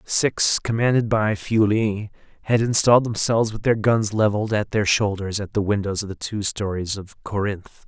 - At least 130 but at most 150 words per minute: No, average, 175 wpm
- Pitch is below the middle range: Yes, low, 105 Hz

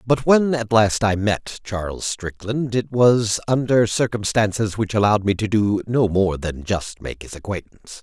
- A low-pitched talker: Yes, low, 110 Hz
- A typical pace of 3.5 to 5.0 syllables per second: Yes, 4.5 syllables/s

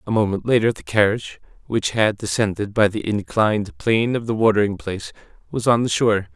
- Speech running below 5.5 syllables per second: No, 6.0 syllables/s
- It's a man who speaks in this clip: Yes, male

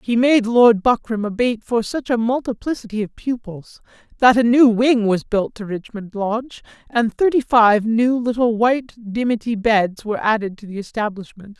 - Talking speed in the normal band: Yes, average, 175 wpm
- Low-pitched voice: No, high, 225 Hz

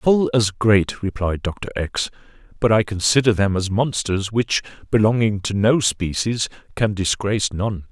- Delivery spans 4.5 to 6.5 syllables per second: No, 4.3 syllables/s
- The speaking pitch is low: Yes, low, 105 Hz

